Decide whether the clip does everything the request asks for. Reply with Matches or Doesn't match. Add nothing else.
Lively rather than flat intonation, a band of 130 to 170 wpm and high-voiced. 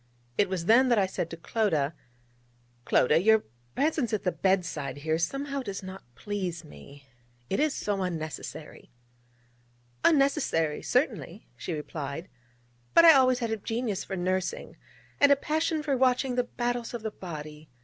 Matches